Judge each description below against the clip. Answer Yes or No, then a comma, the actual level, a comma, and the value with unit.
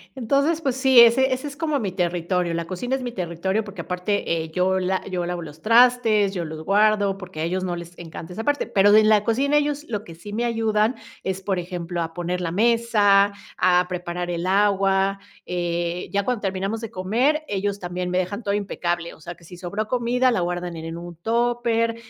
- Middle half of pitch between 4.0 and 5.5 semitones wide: Yes, average, 4.6 semitones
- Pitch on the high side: Yes, high, 195 Hz